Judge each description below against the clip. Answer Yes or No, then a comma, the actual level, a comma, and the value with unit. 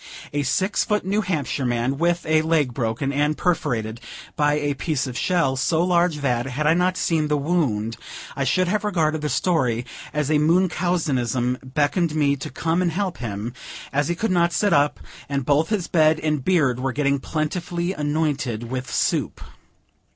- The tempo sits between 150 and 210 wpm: Yes, average, 180 wpm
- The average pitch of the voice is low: No, medium, 150 Hz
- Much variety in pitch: No, average, 4.4 semitones